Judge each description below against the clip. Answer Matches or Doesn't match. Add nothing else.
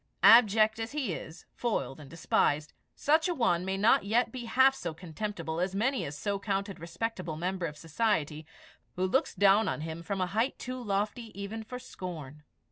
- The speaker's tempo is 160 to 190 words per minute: Matches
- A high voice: Matches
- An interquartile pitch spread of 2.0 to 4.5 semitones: Doesn't match